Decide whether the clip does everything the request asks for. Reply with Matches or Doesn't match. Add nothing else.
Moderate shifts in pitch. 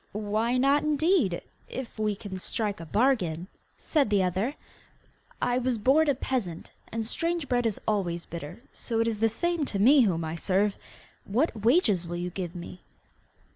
Doesn't match